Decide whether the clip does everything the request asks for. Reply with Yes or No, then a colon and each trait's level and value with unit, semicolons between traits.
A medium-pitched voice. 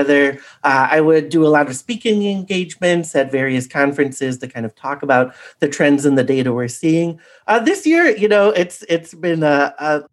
Yes: medium, 150 Hz